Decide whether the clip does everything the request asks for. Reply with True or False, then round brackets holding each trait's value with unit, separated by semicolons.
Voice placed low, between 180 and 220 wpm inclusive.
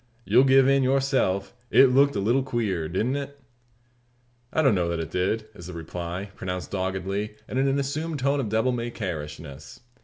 True (110 Hz; 190 wpm)